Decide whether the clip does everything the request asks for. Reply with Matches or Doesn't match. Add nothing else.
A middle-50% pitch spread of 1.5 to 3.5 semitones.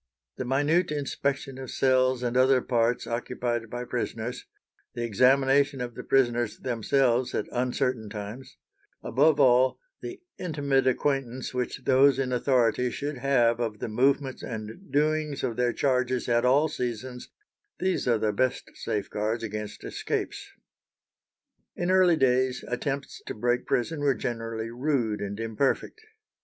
Matches